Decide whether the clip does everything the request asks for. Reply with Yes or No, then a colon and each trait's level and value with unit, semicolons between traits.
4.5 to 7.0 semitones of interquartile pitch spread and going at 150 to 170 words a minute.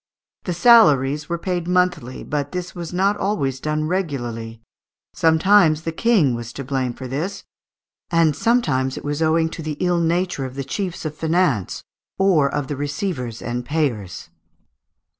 Yes: average, 4.9 semitones; average, 160 wpm